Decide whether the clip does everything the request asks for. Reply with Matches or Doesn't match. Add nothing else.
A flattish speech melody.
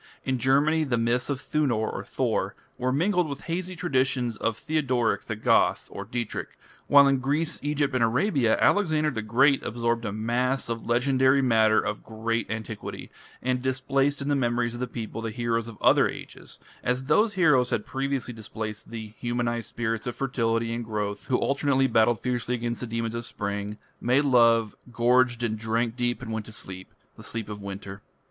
Doesn't match